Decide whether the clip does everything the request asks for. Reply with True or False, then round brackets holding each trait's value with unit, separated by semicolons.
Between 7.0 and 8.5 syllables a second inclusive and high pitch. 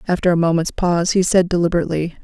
False (7.5 syllables/s; 175 Hz)